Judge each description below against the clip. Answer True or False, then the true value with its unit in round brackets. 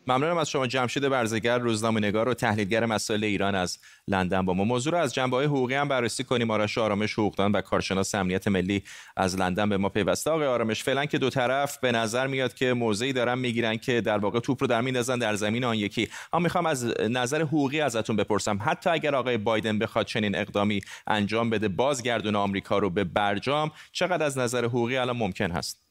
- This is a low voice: True (115 Hz)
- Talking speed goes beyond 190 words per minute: True (205 wpm)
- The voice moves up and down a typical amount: True (3.8 semitones)